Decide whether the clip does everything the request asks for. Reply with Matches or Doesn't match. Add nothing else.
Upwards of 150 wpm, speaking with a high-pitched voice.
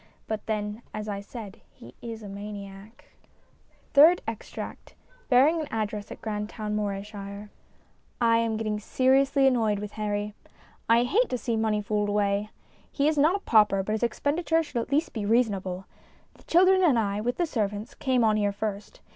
Matches